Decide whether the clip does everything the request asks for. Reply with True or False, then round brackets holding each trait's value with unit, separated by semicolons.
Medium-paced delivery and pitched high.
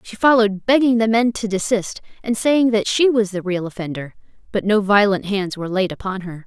False (215 wpm; 205 Hz)